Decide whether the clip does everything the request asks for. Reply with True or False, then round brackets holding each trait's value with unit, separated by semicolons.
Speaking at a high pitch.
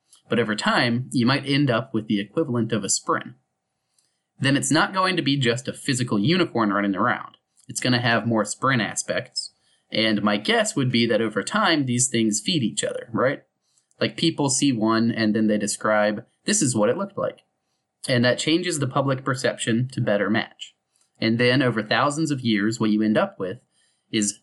False (120 Hz)